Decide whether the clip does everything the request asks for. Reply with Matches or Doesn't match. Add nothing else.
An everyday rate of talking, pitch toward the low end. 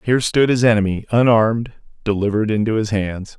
Matches